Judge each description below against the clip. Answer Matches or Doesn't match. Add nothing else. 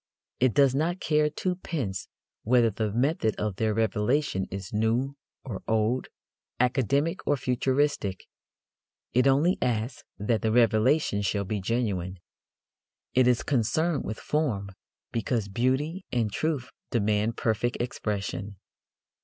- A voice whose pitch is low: Matches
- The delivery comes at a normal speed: Doesn't match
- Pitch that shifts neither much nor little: Matches